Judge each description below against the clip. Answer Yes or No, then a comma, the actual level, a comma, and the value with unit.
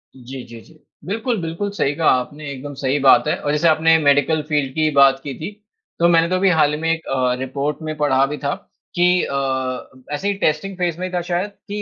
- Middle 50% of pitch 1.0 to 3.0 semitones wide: No, average, 3.7 semitones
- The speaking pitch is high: No, medium, 155 Hz